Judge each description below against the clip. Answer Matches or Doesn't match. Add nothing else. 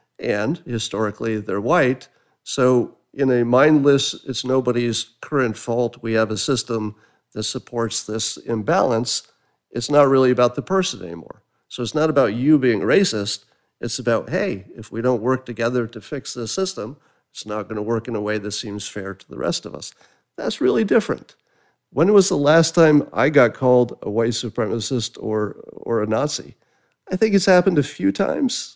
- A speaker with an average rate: Matches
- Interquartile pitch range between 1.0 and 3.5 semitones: Doesn't match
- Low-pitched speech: Matches